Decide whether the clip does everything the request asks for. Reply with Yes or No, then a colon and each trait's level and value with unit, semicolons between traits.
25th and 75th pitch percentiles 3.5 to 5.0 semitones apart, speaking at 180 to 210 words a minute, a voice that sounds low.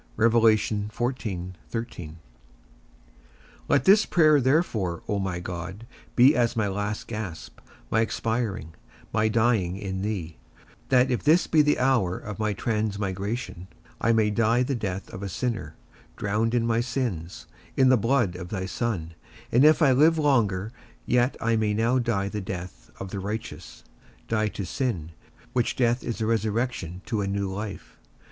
No: average, 4.1 semitones; average, 155 wpm; low, 110 Hz